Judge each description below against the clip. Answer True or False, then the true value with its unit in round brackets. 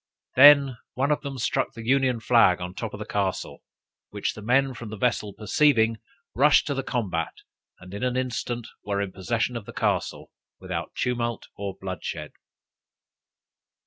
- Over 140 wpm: True (170 wpm)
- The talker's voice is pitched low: True (120 Hz)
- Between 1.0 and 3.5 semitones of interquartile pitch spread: False (4.4 semitones)